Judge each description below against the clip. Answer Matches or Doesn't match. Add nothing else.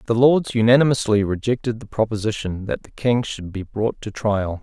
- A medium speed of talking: Matches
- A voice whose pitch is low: Matches